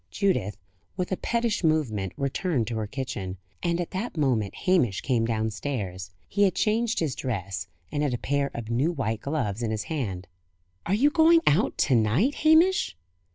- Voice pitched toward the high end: No, medium, 140 Hz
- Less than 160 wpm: No, average, 175 wpm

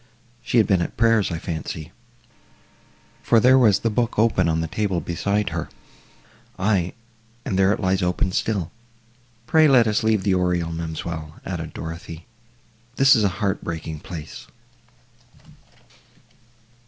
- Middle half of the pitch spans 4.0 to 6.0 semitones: Yes, average, 4.6 semitones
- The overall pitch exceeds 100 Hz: No, very low, 95 Hz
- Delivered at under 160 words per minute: Yes, average, 140 wpm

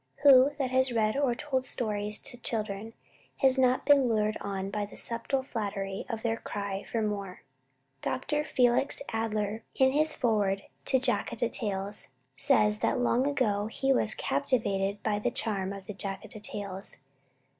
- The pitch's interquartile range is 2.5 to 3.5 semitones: No, average, 4.0 semitones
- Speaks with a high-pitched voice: Yes, high, 220 Hz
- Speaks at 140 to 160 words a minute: Yes, average, 155 wpm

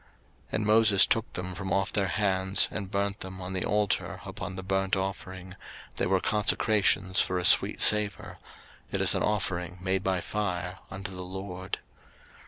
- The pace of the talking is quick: No, average, 175 wpm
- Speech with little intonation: Yes, narrow, 1.7 semitones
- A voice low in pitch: Yes, very low, 95 Hz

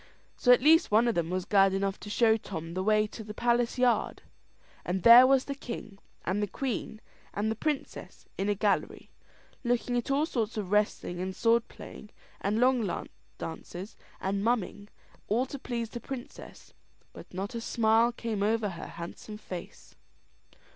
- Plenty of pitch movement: No, average, 3.5 semitones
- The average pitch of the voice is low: No, high, 220 Hz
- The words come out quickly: No, average, 175 wpm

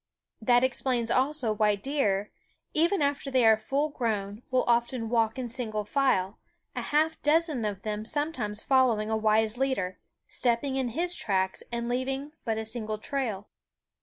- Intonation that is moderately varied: Yes, average, 3.9 semitones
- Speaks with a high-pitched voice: Yes, high, 240 Hz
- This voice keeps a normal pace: Yes, average, 160 wpm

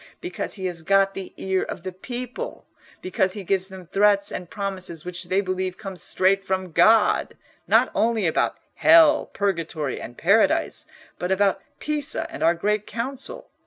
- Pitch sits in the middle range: No, high, 195 Hz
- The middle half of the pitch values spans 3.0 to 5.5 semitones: No, narrow, 2.6 semitones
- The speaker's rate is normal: Yes, average, 160 wpm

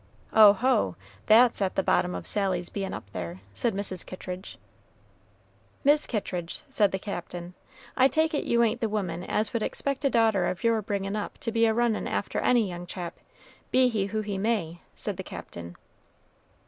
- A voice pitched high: Yes, high, 205 Hz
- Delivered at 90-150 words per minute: No, average, 180 wpm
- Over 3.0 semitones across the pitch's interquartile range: Yes, average, 4.1 semitones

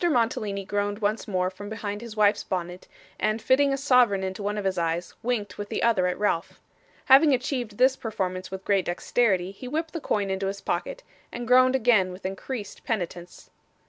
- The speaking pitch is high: Yes, high, 205 Hz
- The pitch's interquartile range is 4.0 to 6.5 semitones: Yes, average, 4.5 semitones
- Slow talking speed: No, average, 190 wpm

